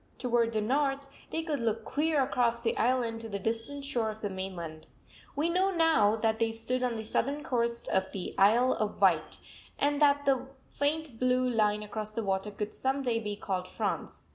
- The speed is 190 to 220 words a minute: Yes, average, 195 wpm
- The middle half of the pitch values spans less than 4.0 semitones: No, average, 4.5 semitones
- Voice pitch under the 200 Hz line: No, high, 235 Hz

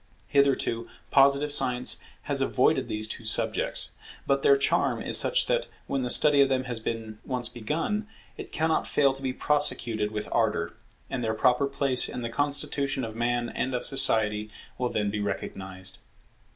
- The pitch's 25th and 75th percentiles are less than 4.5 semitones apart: Yes, average, 3.9 semitones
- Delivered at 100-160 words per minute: No, average, 170 wpm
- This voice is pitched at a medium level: No, low, 125 Hz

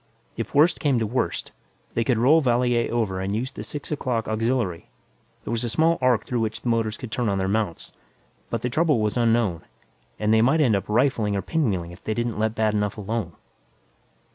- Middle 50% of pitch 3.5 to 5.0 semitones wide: No, average, 3.0 semitones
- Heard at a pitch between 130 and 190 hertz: No, low, 115 Hz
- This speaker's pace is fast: Yes, fast, 210 wpm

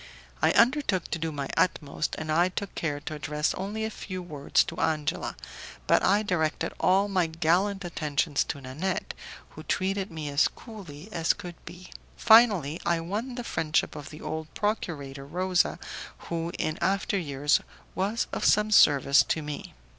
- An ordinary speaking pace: Yes, average, 165 wpm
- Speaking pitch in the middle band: Yes, medium, 170 Hz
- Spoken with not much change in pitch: No, average, 4.5 semitones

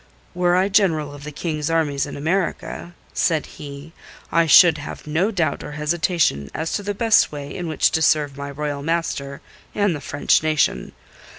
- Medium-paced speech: Yes, average, 180 wpm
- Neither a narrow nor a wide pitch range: Yes, average, 3.2 semitones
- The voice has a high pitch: No, medium, 155 Hz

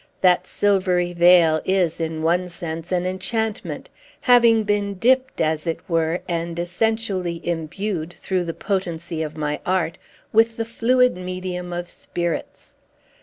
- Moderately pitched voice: Yes, medium, 180 Hz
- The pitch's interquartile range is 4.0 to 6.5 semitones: No, average, 3.3 semitones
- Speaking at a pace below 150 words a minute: Yes, slow, 135 wpm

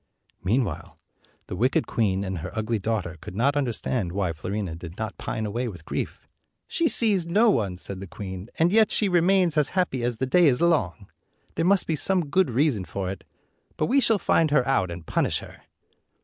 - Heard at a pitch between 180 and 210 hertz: No, low, 120 Hz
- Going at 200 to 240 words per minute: Yes, fast, 205 wpm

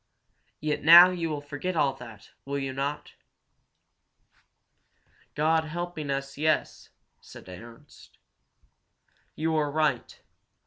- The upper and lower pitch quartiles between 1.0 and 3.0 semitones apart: Yes, narrow, 2.6 semitones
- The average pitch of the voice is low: No, medium, 150 Hz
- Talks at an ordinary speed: No, slow, 105 wpm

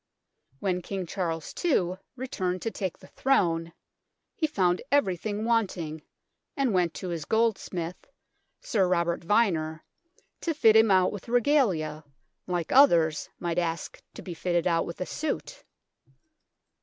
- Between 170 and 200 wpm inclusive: No, slow, 135 wpm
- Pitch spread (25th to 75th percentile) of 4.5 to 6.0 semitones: Yes, average, 4.8 semitones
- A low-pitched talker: No, medium, 185 Hz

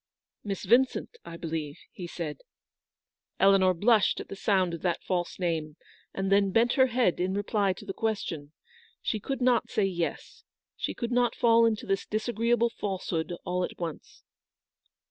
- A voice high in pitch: Yes, high, 195 Hz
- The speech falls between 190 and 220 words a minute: No, average, 170 wpm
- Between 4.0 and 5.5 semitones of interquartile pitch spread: Yes, average, 4.7 semitones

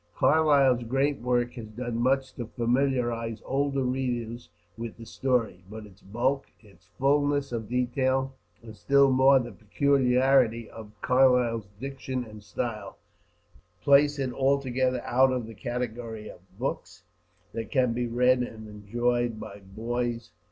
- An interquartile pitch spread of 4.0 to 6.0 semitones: No, narrow, 2.6 semitones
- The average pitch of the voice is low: Yes, low, 125 Hz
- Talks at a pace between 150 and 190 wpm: No, slow, 135 wpm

